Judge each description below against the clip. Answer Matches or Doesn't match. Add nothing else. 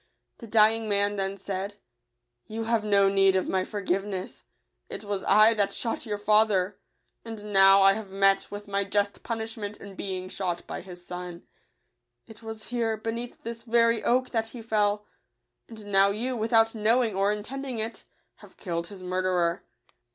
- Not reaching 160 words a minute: Doesn't match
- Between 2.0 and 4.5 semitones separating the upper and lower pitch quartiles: Matches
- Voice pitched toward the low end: Doesn't match